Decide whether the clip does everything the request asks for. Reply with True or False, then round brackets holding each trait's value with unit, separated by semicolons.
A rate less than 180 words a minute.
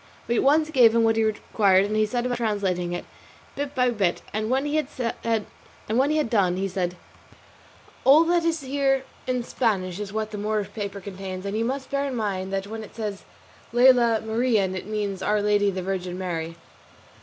False (190 wpm)